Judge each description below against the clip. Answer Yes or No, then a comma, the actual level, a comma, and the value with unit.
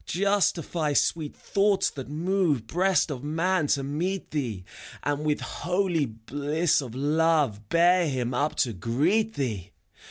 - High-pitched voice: No, medium, 150 Hz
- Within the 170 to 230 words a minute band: No, slow, 135 wpm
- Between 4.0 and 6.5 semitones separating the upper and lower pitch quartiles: Yes, average, 4.9 semitones